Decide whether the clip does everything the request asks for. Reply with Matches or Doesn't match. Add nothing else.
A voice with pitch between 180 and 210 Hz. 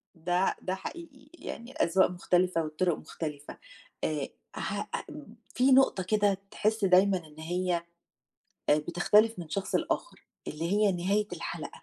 Matches